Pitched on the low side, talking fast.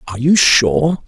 No: low, 130 Hz; average, 165 wpm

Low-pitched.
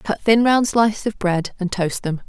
No: high, 205 Hz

